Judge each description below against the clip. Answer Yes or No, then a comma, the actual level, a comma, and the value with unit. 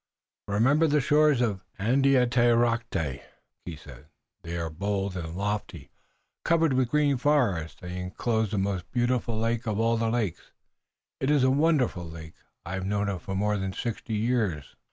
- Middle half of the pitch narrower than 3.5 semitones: No, average, 5.0 semitones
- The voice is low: Yes, low, 110 Hz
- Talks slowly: No, average, 155 wpm